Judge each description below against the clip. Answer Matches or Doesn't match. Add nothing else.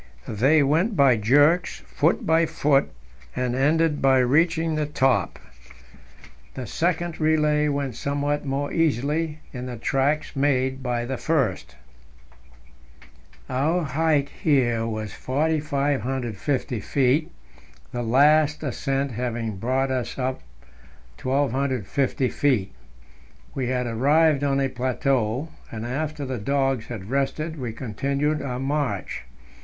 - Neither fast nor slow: Doesn't match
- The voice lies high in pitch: Doesn't match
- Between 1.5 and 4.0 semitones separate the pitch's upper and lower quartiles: Matches